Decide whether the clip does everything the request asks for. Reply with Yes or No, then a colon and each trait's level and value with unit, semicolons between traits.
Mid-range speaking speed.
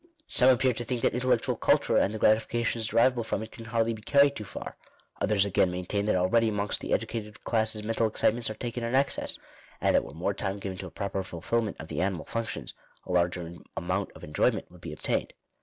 No: fast, 220 wpm